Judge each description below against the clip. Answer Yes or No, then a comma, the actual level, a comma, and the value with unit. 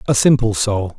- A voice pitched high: No, low, 115 Hz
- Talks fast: No, average, 185 wpm